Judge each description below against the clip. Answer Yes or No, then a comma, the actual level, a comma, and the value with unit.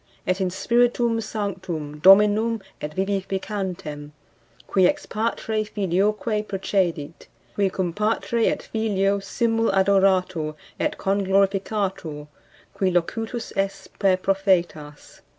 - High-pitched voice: Yes, high, 195 Hz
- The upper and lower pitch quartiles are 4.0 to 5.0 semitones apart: No, narrow, 2.5 semitones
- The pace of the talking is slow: Yes, slow, 100 wpm